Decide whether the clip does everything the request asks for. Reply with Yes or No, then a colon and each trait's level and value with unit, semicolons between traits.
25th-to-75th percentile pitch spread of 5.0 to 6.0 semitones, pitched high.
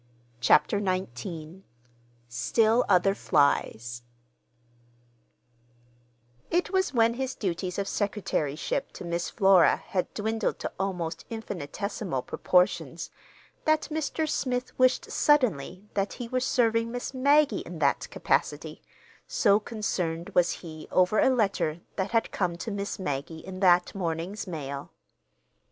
Yes: average, 5.3 semitones; high, 195 Hz